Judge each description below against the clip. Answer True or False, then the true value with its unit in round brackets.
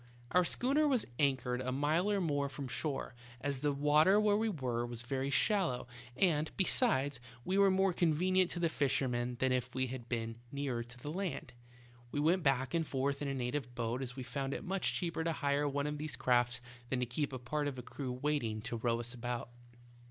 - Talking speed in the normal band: False (210 wpm)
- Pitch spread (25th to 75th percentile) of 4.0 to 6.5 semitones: True (4.6 semitones)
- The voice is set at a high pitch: False (140 Hz)